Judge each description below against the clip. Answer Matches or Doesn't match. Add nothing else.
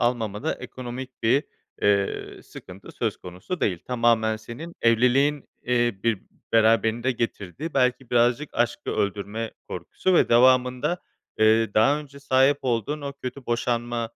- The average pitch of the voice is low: Matches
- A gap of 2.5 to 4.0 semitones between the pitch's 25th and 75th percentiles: Matches